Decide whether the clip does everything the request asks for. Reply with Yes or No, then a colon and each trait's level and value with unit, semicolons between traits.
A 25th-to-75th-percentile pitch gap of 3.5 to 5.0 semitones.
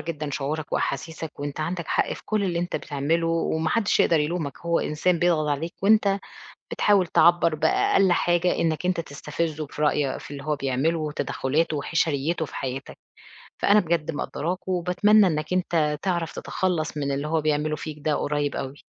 No: average, 2.7 semitones